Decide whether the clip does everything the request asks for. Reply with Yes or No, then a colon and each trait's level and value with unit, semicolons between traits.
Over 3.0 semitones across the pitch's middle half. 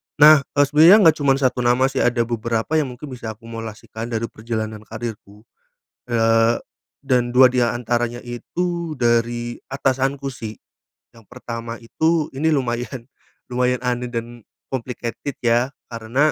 No: narrow, 2.6 semitones